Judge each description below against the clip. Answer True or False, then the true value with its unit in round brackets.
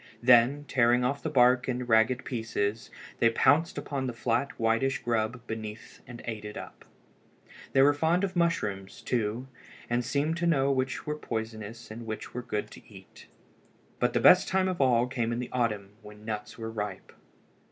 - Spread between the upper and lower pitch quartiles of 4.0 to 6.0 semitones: False (3.2 semitones)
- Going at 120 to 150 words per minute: False (180 wpm)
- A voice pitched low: True (120 Hz)